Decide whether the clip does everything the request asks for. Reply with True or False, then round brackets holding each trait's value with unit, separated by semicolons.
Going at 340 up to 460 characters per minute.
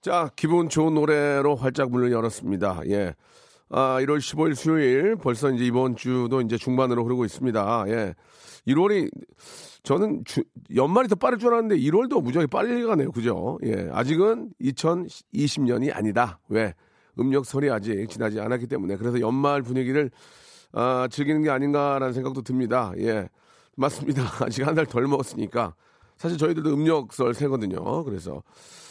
False (325 characters per minute)